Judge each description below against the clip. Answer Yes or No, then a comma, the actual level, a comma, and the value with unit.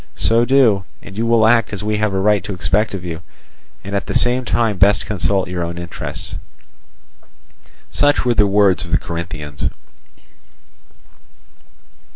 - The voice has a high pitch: No, low, 100 Hz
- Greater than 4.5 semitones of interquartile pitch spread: No, average, 3.8 semitones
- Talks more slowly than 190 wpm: Yes, average, 160 wpm